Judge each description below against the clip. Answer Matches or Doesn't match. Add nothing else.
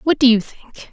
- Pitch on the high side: Matches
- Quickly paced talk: Matches